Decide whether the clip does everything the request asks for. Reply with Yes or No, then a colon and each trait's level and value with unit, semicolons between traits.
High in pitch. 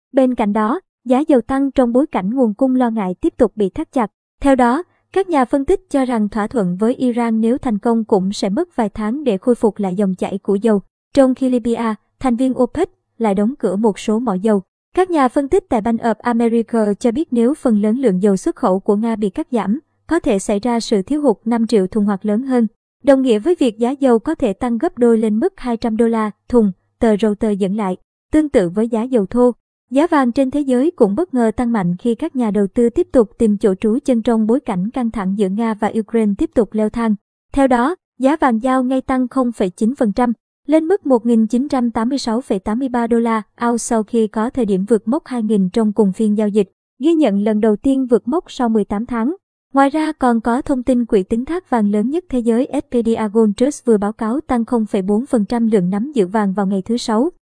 Yes: high, 235 Hz